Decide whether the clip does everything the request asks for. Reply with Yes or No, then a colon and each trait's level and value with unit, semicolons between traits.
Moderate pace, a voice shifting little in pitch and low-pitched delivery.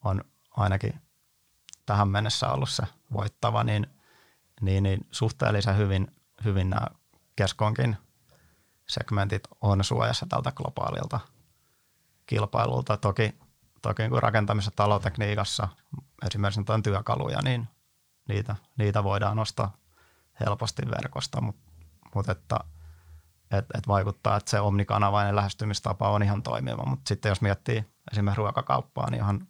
Yes: average, 115 wpm; narrow, 2.0 semitones; low, 105 Hz